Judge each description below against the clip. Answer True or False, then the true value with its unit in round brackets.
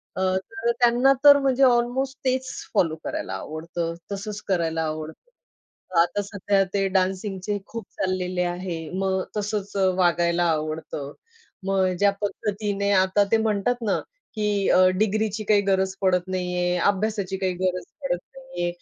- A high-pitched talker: True (195 Hz)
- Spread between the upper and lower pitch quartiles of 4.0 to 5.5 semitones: False (3.2 semitones)